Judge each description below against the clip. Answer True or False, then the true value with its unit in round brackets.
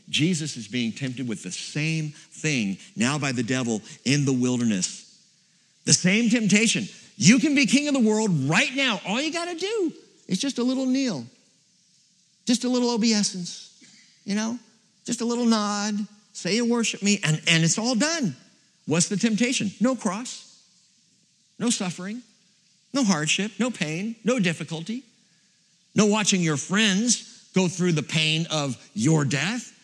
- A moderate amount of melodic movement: False (5.8 semitones)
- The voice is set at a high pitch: True (205 Hz)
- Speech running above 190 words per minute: False (160 wpm)